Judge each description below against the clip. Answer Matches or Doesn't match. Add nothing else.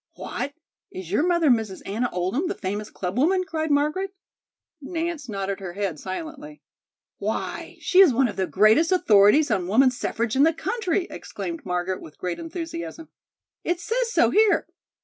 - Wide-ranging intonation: Matches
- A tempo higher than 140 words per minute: Matches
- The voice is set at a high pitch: Matches